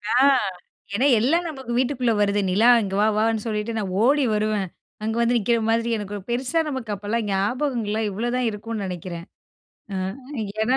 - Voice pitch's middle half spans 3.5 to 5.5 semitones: No, average, 3.1 semitones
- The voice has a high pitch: Yes, high, 225 Hz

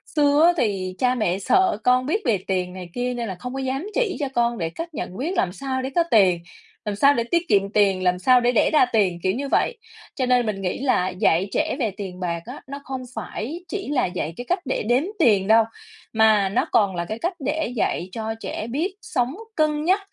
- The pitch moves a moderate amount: No, wide, 6.5 semitones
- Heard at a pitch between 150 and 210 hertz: No, high, 235 Hz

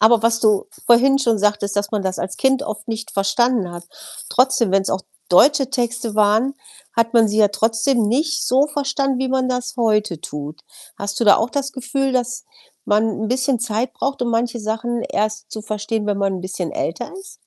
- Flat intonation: No, average, 3.6 semitones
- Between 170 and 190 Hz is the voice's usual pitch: No, high, 230 Hz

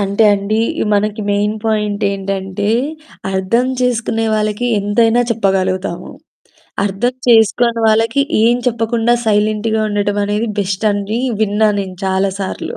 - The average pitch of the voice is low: No, high, 210 Hz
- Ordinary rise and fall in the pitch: No, narrow, 2.2 semitones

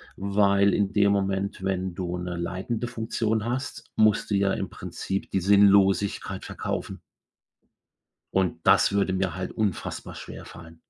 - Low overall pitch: Yes, low, 100 Hz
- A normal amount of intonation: No, narrow, 1.5 semitones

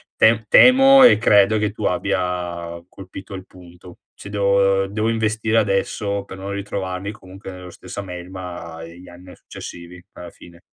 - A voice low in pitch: Yes, very low, 95 Hz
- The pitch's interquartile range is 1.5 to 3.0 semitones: Yes, narrow, 2.4 semitones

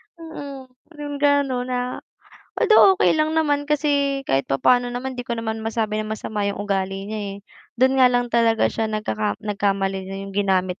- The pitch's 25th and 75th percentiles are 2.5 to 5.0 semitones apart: No, wide, 5.4 semitones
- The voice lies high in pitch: Yes, high, 235 Hz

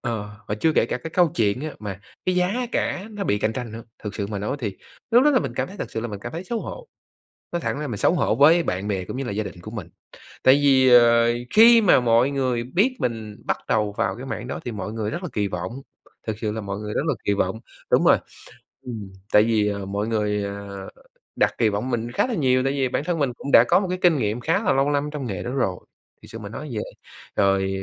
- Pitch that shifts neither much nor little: No, wide, 5.7 semitones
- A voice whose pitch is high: No, low, 115 Hz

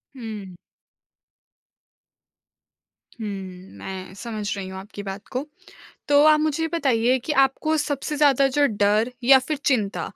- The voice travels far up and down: Yes, wide, 6.0 semitones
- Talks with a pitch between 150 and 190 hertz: No, very high, 250 Hz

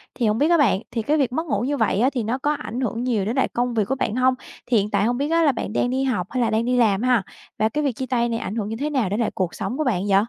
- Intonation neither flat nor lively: Yes, average, 3.4 semitones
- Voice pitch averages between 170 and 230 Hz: No, high, 245 Hz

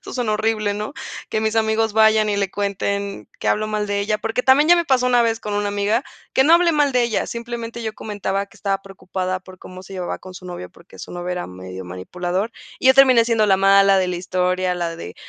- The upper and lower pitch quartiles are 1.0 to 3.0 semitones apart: No, average, 3.5 semitones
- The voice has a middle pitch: No, high, 205 Hz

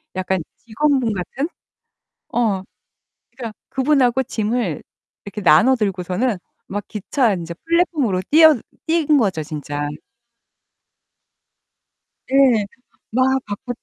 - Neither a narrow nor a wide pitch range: No, wide, 5.7 semitones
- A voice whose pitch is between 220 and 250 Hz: Yes, high, 230 Hz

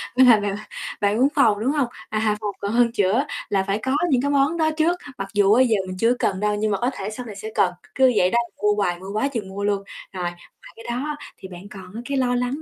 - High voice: Yes, high, 215 Hz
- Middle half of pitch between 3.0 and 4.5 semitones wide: Yes, average, 4.0 semitones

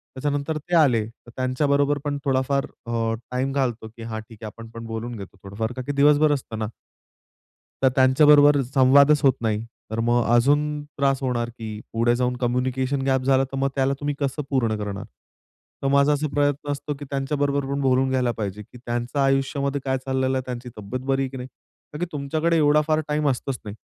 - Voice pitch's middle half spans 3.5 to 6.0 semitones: No, average, 3.1 semitones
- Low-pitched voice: Yes, low, 130 Hz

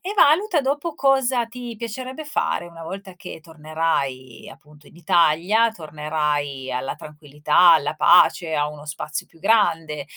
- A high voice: No, medium, 165 Hz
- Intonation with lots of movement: Yes, wide, 7.5 semitones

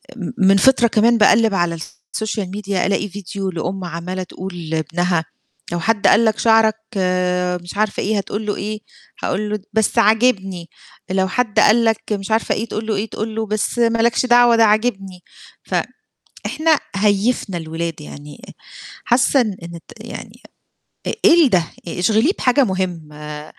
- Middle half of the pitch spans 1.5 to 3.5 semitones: No, average, 3.9 semitones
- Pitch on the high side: Yes, high, 205 Hz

